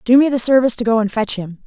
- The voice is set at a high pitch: Yes, high, 230 Hz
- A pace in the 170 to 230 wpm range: No, fast, 325 wpm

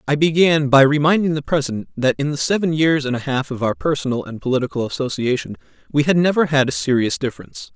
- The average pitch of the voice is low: No, medium, 145 Hz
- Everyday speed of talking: No, fast, 210 wpm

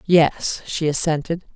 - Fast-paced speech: No, slow, 115 wpm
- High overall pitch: No, medium, 160 Hz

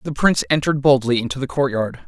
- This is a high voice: No, low, 135 Hz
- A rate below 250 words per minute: Yes, average, 200 wpm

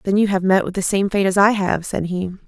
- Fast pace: Yes, fast, 315 wpm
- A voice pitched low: No, high, 190 Hz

